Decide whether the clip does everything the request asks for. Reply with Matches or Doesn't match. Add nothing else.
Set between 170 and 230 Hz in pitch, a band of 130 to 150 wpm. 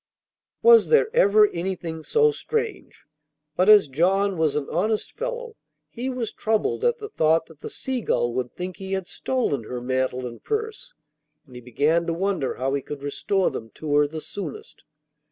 Doesn't match